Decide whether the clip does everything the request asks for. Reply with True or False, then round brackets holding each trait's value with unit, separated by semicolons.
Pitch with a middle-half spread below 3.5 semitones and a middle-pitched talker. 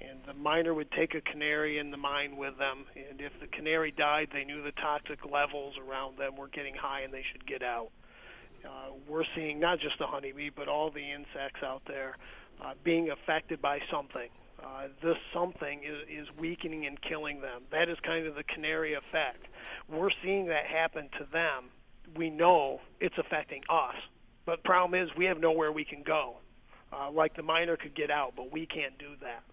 True (2.4 semitones; 150 Hz)